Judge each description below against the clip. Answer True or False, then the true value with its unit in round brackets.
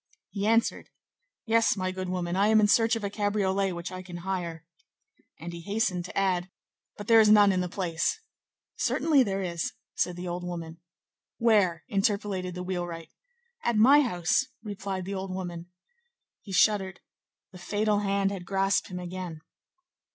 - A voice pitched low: False (190 Hz)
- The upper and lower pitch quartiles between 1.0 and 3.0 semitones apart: True (2.6 semitones)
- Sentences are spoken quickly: False (165 wpm)